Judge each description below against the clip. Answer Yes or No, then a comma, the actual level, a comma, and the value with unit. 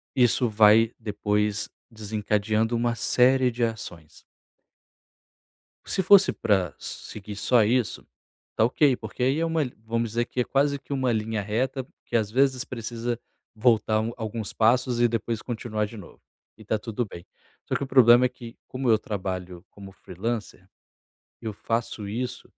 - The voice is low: Yes, low, 115 Hz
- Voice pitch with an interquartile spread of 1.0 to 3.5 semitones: Yes, average, 2.8 semitones